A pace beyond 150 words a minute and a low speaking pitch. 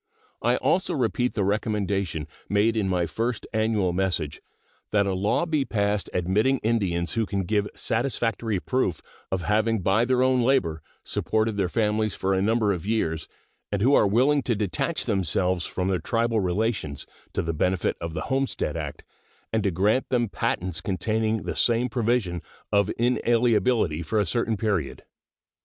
Yes: average, 165 wpm; low, 105 Hz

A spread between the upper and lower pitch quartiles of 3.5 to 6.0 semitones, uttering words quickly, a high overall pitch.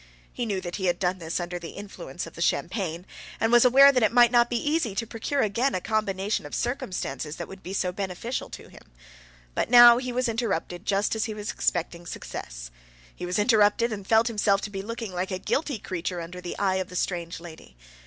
Yes: average, 4.6 semitones; fast, 225 wpm; high, 200 Hz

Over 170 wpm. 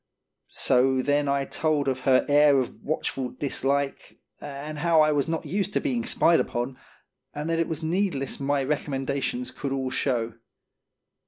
No: average, 160 wpm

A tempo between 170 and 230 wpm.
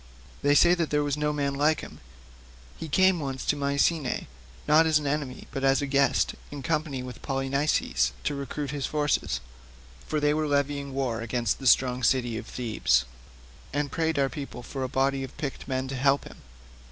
Yes: average, 190 wpm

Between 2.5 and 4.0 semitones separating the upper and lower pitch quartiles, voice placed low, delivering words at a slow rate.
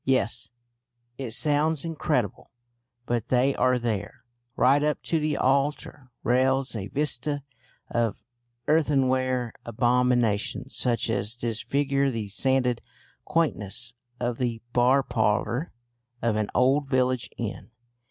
Yes: average, 2.8 semitones; low, 125 Hz; slow, 115 wpm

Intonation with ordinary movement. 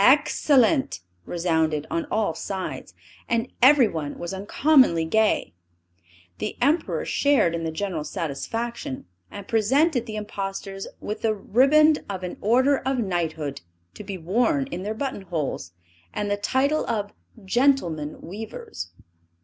No: wide, 7.3 semitones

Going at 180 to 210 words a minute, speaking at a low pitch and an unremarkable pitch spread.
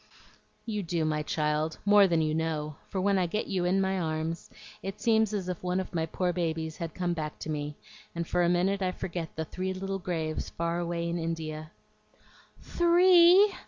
No: average, 195 wpm; medium, 175 Hz; average, 3.2 semitones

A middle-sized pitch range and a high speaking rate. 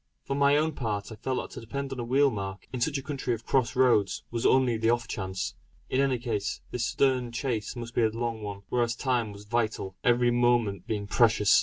Yes: average, 3.1 semitones; fast, 225 wpm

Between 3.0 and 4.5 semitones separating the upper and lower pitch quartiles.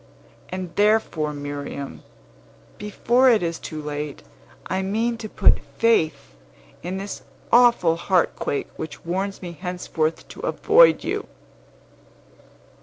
No: wide, 5.4 semitones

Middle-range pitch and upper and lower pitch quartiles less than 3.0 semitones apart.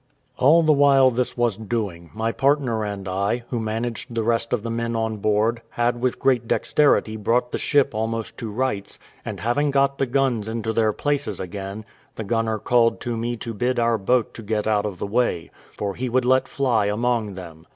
No: low, 115 Hz; narrow, 2.6 semitones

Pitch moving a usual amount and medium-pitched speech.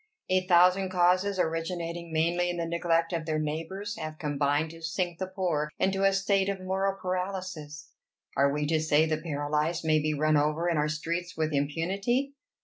Yes: average, 3.2 semitones; medium, 165 Hz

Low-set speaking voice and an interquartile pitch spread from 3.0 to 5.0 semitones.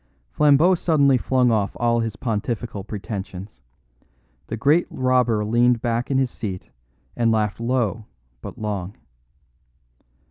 Yes: low, 115 Hz; average, 3.3 semitones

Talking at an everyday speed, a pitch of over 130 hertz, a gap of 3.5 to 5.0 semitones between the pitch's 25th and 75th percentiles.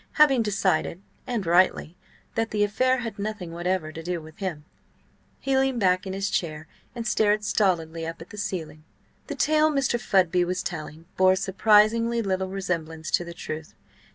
Yes: average, 170 wpm; high, 190 Hz; average, 4.5 semitones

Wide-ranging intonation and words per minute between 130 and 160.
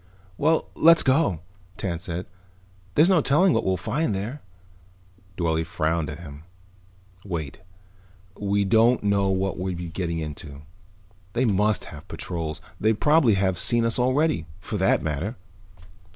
Yes: wide, 6.5 semitones; average, 145 wpm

